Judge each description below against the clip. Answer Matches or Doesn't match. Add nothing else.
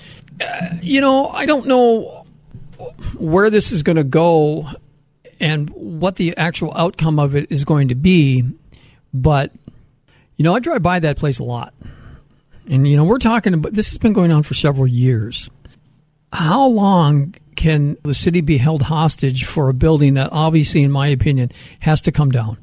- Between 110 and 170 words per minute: Doesn't match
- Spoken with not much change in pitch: Doesn't match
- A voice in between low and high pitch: Matches